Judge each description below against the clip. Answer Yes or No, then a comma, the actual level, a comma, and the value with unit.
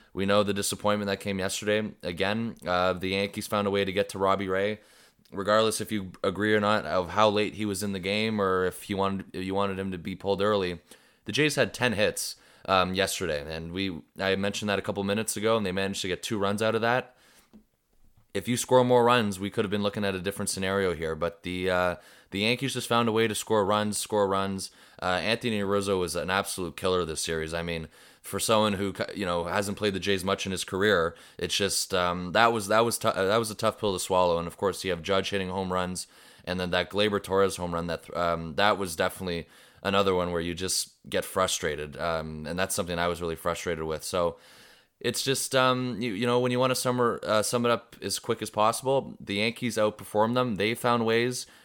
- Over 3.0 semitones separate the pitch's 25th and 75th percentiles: No, average, 2.7 semitones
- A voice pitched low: Yes, low, 100 Hz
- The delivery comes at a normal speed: No, fast, 235 wpm